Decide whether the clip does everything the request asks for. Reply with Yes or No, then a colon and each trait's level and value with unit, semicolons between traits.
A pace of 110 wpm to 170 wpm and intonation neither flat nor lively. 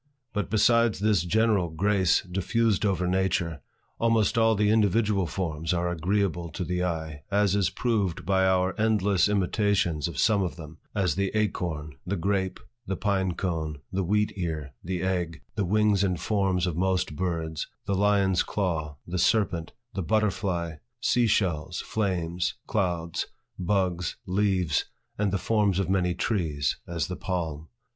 Yes: average, 150 wpm; average, 3.2 semitones